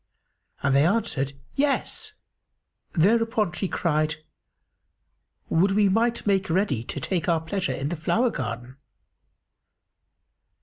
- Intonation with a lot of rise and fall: Yes, wide, 6.0 semitones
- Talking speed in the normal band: No, slow, 115 wpm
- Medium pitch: Yes, medium, 180 Hz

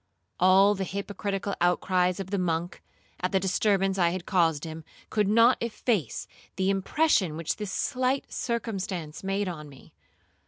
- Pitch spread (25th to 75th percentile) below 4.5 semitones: Yes, average, 2.7 semitones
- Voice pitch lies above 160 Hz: Yes, high, 190 Hz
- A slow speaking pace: No, average, 155 wpm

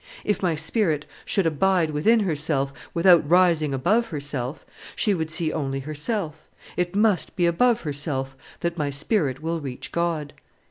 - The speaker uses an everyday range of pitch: Yes, average, 3.8 semitones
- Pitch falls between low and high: Yes, medium, 160 Hz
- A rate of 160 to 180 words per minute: No, average, 150 wpm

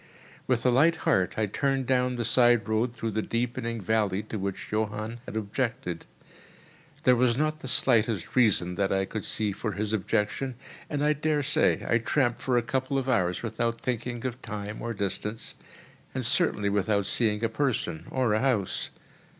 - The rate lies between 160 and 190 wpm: Yes, average, 175 wpm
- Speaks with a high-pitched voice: No, low, 115 Hz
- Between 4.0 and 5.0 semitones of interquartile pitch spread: No, average, 3.3 semitones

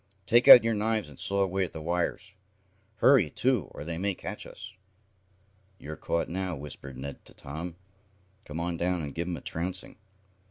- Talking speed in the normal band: Yes, average, 185 wpm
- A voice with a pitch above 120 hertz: No, very low, 90 Hz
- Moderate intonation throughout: Yes, average, 3.7 semitones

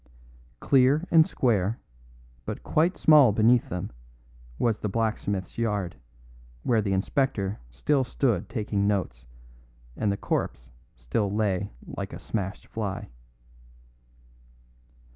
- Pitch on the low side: Yes, low, 105 Hz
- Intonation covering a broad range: No, average, 4.1 semitones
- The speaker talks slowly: Yes, slow, 110 wpm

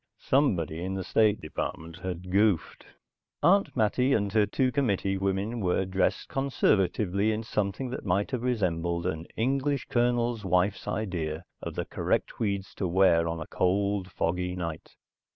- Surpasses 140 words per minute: Yes, average, 150 wpm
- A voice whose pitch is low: Yes, low, 100 Hz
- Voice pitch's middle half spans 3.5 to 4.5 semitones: Yes, average, 3.9 semitones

